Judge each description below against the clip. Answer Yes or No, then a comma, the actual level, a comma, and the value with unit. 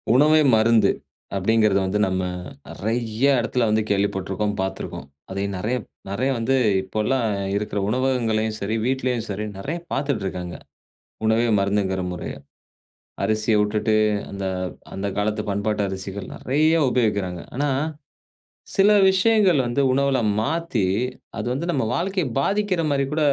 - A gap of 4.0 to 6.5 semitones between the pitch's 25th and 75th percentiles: Yes, average, 5.2 semitones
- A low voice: Yes, low, 110 Hz